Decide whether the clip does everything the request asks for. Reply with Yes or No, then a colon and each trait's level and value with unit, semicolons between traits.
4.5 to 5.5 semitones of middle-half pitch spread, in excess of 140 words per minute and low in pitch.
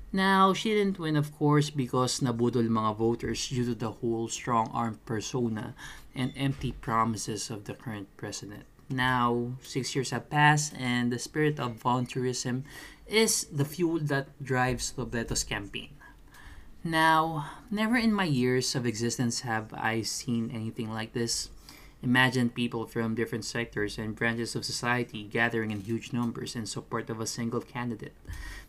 No: average, 3.1 semitones; fast, 155 wpm; low, 120 Hz